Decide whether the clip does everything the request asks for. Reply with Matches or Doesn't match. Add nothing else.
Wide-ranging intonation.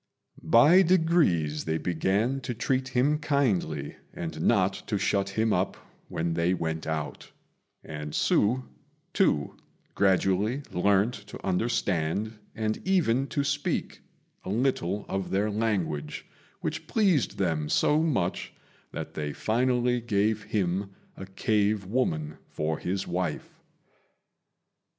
Matches